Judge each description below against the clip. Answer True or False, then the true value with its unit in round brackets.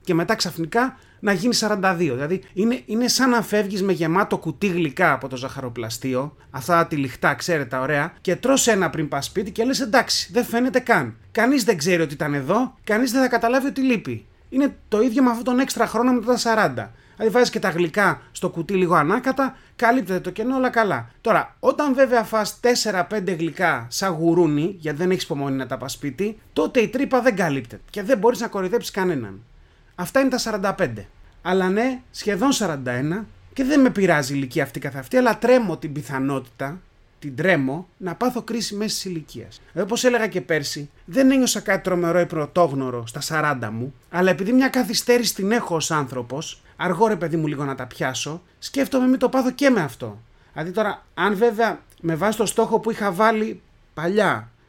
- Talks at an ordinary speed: False (190 wpm)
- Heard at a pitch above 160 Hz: True (190 Hz)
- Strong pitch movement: True (7.5 semitones)